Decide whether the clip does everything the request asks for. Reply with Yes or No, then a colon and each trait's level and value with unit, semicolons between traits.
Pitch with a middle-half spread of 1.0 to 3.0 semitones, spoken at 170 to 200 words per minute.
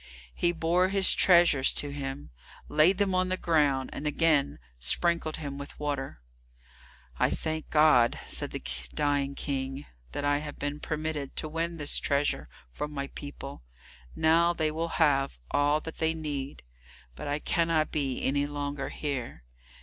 No: narrow, 2.5 semitones; average, 155 wpm